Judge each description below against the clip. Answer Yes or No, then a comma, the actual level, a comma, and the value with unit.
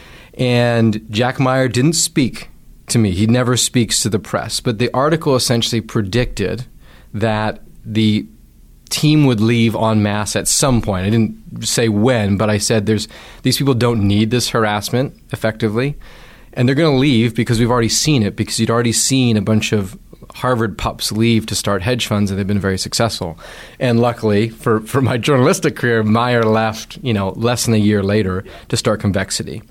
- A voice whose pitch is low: Yes, low, 115 Hz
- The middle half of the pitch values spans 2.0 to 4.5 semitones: Yes, narrow, 2.5 semitones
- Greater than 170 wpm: Yes, average, 180 wpm